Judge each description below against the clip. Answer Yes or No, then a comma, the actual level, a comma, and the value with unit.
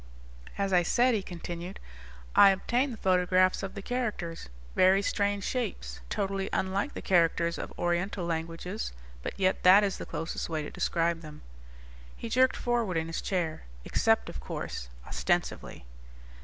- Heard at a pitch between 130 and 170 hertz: No, medium, 185 Hz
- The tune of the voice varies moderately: Yes, average, 3.1 semitones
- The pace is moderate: Yes, average, 155 wpm